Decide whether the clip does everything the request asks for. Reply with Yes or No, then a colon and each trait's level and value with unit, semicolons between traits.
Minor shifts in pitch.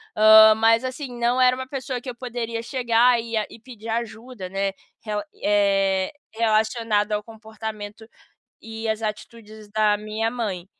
Yes: narrow, 1.9 semitones